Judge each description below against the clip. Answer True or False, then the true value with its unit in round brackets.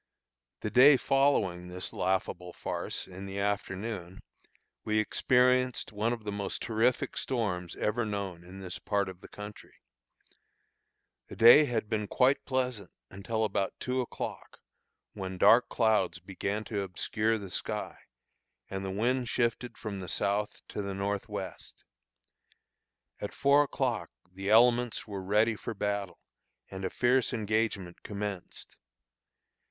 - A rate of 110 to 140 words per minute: True (135 wpm)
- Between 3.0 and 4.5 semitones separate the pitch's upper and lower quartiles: True (3.3 semitones)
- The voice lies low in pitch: True (105 Hz)